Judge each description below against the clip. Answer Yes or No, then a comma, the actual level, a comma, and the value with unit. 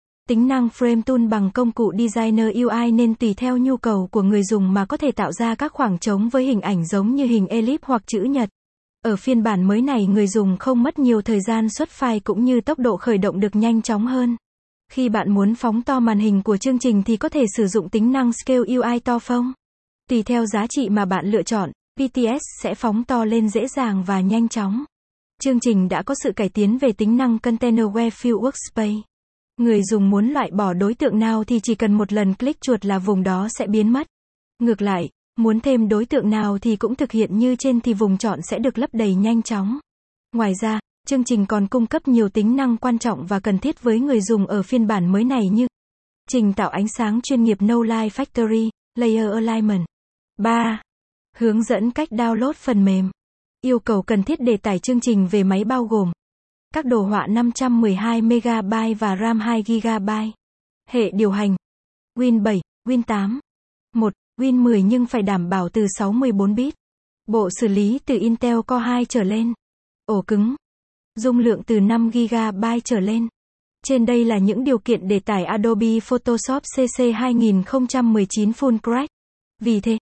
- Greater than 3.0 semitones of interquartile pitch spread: No, narrow, 2.6 semitones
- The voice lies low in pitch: No, high, 230 Hz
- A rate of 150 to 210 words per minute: Yes, average, 200 wpm